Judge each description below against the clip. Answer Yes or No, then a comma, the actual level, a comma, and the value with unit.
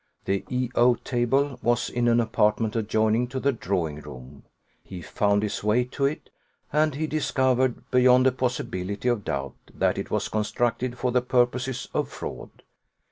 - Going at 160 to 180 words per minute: Yes, average, 165 wpm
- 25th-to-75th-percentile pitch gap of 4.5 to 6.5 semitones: No, average, 3.3 semitones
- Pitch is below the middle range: Yes, low, 120 Hz